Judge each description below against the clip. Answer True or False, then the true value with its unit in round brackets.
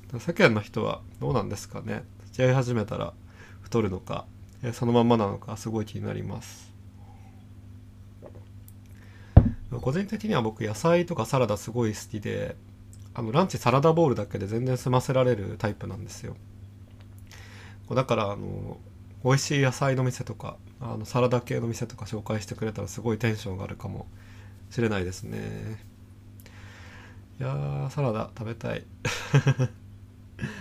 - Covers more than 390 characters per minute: False (300 characters per minute)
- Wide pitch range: False (3.5 semitones)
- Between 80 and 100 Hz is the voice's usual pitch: False (110 Hz)